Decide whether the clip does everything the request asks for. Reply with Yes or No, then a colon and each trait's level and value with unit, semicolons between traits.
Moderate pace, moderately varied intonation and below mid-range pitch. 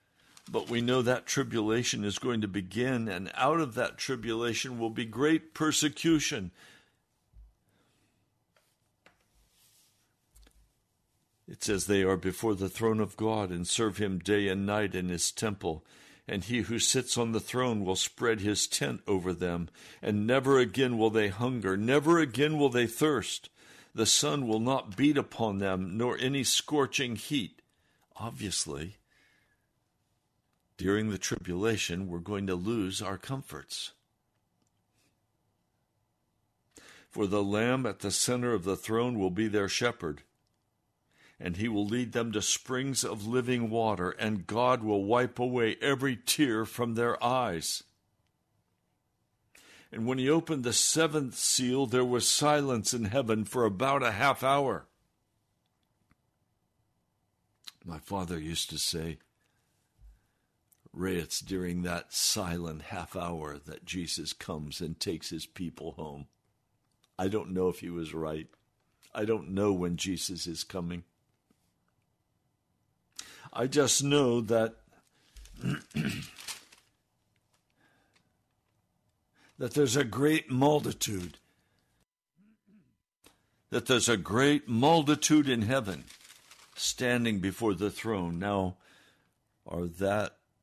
No: slow, 125 wpm; average, 5.0 semitones; low, 110 Hz